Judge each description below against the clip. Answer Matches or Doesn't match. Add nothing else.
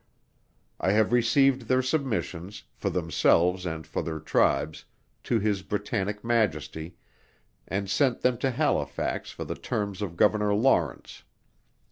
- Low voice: Matches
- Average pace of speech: Doesn't match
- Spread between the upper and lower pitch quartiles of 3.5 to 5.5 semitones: Matches